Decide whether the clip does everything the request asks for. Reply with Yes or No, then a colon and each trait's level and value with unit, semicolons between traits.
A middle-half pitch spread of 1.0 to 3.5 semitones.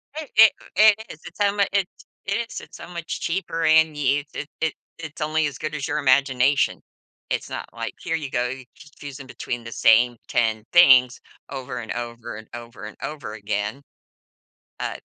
No: average, 4.9 semitones